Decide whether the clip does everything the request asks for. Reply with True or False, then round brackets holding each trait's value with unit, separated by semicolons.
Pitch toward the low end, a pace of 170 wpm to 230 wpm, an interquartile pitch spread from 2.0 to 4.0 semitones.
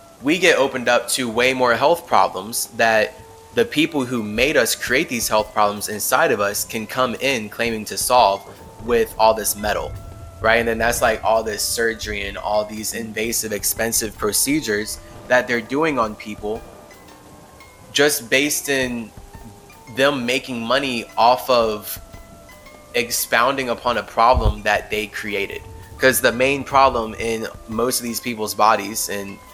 False (110 Hz; 155 wpm; 3.2 semitones)